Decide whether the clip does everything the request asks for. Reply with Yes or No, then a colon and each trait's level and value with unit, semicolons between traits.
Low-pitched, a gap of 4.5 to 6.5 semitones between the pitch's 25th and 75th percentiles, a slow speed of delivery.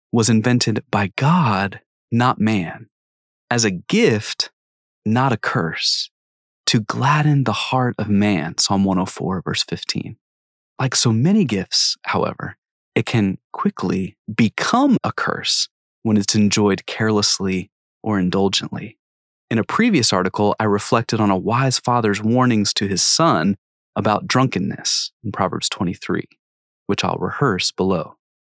No: low, 105 Hz; average, 4.0 semitones; slow, 130 wpm